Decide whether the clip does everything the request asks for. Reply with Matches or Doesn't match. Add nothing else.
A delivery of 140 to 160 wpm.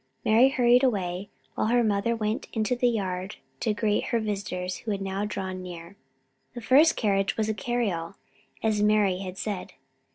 Doesn't match